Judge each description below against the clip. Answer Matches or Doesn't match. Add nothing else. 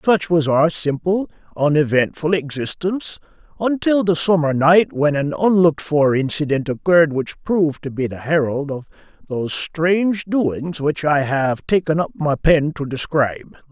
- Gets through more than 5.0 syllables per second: Doesn't match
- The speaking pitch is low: Doesn't match